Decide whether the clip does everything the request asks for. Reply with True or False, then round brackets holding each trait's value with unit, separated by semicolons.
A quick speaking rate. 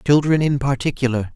False (135 wpm)